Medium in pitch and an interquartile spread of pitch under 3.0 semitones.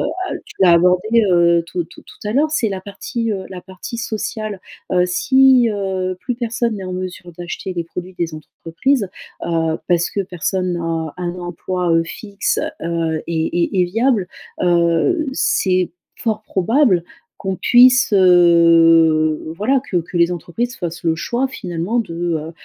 No: medium, 180 Hz; average, 4.2 semitones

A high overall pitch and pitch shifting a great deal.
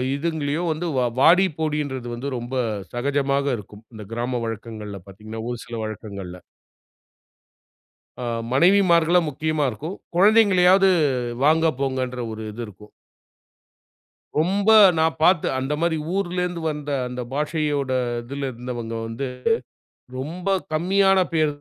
No: medium, 145 Hz; wide, 6.0 semitones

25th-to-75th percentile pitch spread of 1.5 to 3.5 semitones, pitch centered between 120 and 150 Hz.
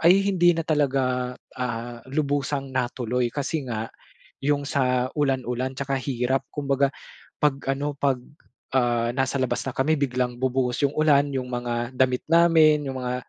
Yes: narrow, 2.4 semitones; low, 135 Hz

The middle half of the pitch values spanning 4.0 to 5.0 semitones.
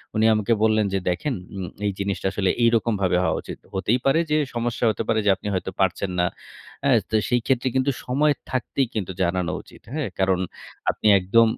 Yes: average, 4.4 semitones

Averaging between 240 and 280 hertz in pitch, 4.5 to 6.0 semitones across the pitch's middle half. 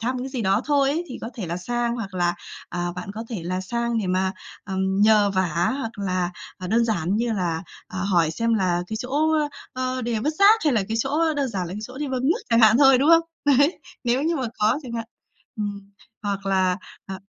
No: high, 220 Hz; average, 5.2 semitones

